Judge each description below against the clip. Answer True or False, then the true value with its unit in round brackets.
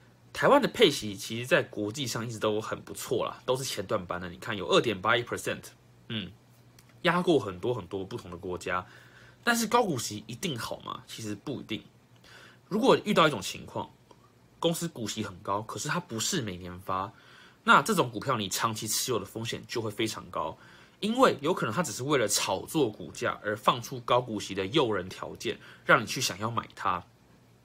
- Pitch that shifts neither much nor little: True (3.7 semitones)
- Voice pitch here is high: False (110 Hz)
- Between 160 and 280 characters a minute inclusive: False (295 characters per minute)